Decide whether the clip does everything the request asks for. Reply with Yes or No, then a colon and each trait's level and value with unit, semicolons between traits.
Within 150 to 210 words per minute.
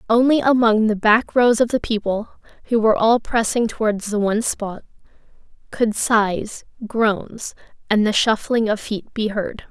Yes: average, 160 wpm